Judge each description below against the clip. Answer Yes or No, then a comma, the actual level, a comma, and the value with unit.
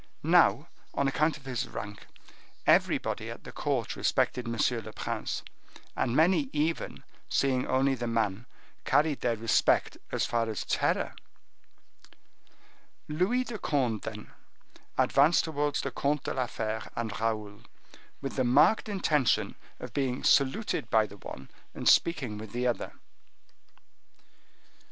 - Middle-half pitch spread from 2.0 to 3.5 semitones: No, average, 4.7 semitones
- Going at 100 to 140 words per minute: Yes, slow, 135 wpm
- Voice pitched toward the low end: Yes, low, 130 Hz